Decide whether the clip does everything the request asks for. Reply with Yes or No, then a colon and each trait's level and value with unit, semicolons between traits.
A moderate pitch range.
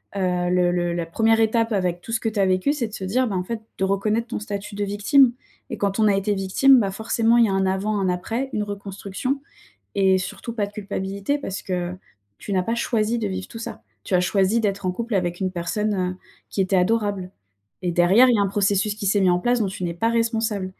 Yes: average, 3.1 semitones